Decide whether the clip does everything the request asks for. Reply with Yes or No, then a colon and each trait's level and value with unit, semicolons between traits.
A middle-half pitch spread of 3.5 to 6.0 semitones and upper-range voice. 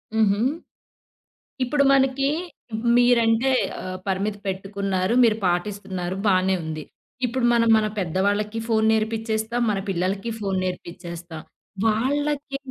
Yes: average, 3.8 semitones; high, 210 Hz